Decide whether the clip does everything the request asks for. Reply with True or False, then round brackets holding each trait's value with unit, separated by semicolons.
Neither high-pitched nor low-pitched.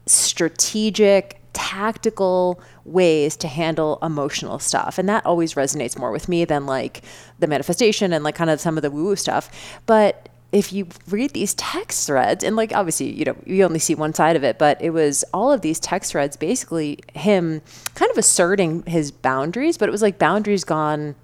True (170 Hz)